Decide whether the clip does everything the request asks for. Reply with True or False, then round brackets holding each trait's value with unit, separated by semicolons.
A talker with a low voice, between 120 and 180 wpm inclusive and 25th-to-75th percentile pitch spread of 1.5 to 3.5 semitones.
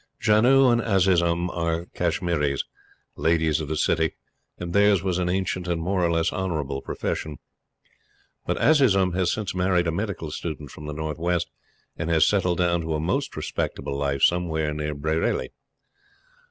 True (85 Hz; 160 wpm; 2.9 semitones)